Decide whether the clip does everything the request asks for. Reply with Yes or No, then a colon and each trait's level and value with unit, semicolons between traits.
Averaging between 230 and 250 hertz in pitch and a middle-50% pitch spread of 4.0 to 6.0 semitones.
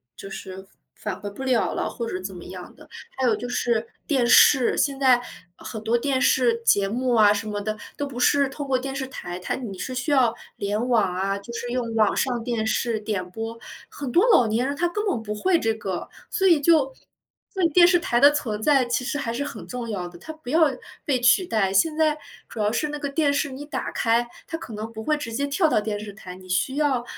Yes: high, 240 Hz; average, 4.8 semitones